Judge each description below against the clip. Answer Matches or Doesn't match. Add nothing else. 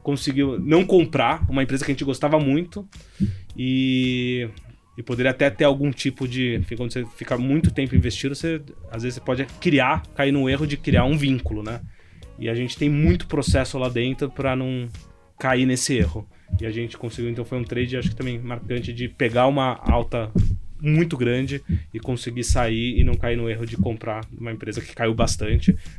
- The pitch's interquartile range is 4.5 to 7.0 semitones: Doesn't match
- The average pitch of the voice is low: Matches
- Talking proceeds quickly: Matches